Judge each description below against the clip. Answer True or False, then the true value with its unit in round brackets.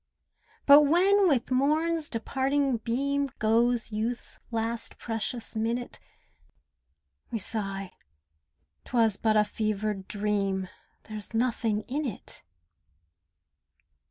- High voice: True (230 Hz)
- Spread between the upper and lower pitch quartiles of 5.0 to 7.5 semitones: False (4.1 semitones)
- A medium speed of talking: False (95 wpm)